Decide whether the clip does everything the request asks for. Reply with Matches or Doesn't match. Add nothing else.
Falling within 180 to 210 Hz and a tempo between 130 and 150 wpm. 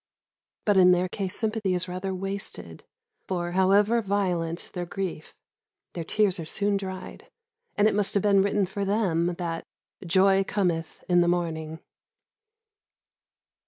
Matches